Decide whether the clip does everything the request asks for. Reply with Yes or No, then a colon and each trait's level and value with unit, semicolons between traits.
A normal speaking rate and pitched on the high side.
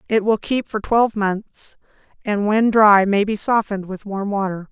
Yes: average, 190 wpm; high, 205 Hz